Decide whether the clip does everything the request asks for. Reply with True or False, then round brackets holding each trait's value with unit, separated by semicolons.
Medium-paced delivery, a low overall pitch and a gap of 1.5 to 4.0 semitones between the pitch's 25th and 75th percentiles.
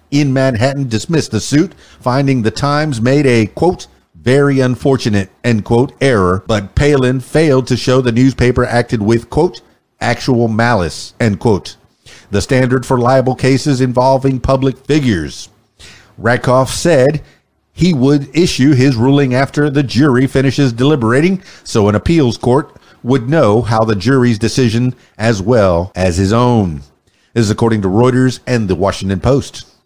True (150 wpm; 125 Hz; 3.3 semitones)